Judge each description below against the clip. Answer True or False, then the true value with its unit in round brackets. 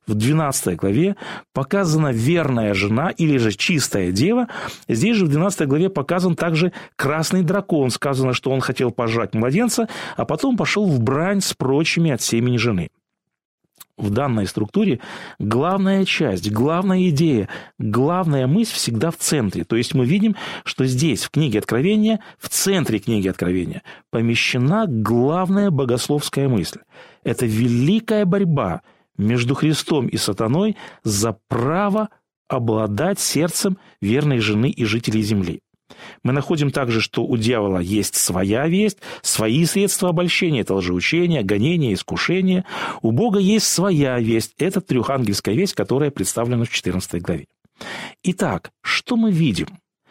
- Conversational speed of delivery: True (135 wpm)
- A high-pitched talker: False (140 Hz)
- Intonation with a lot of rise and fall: True (8.2 semitones)